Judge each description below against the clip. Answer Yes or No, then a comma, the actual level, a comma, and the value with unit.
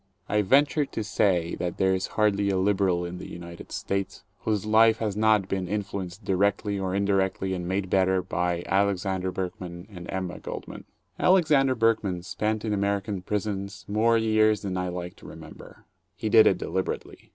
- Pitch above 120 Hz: No, low, 100 Hz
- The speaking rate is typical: Yes, average, 170 wpm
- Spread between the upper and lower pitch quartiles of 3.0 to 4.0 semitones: No, narrow, 2.5 semitones